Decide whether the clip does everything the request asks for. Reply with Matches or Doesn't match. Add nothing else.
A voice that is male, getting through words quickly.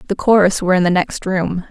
Doesn't match